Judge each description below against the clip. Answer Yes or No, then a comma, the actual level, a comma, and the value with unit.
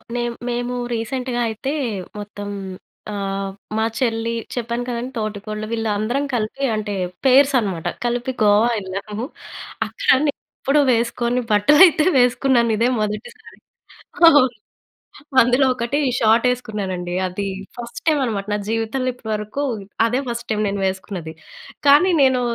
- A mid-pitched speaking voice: No, high, 235 Hz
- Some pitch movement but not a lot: Yes, average, 3.1 semitones